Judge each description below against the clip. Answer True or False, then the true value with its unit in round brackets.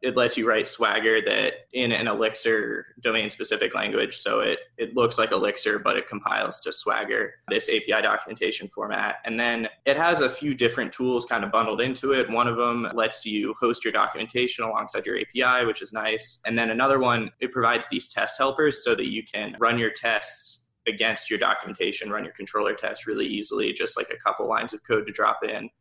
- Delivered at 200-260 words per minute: True (205 wpm)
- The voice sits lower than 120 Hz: False (135 Hz)